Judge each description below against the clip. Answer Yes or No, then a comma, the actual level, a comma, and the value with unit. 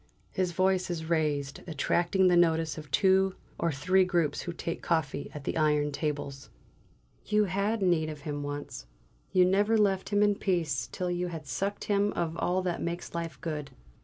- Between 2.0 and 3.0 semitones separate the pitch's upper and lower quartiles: No, average, 3.8 semitones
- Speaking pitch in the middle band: Yes, medium, 170 Hz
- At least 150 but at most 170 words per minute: No, average, 180 wpm